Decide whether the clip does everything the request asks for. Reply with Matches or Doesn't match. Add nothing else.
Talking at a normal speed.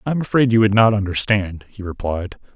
Doesn't match